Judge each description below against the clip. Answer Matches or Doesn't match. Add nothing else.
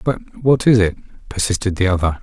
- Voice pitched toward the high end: Doesn't match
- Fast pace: Doesn't match